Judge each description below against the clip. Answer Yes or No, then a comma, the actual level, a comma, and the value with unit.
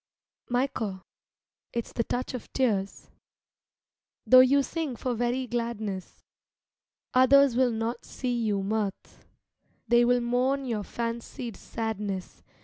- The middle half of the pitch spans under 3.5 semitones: Yes, narrow, 2.6 semitones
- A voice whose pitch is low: No, high, 240 Hz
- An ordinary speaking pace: No, slow, 120 wpm